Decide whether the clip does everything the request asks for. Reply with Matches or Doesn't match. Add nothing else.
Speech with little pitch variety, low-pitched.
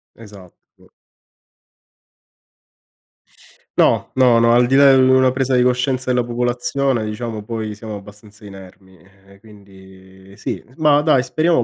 Doesn't match